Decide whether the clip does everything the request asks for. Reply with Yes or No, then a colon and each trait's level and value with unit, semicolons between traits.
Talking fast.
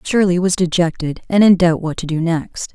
Yes: fast, 220 wpm